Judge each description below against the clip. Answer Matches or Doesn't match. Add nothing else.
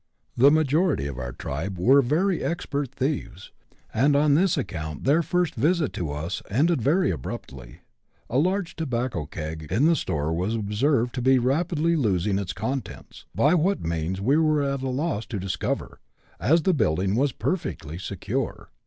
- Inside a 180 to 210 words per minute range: Doesn't match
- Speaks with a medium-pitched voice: Doesn't match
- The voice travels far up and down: Matches